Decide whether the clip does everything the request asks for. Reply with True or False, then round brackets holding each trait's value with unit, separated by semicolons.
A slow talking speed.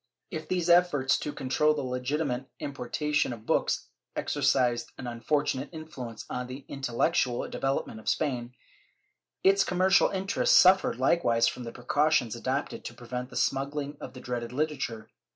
False (150 wpm)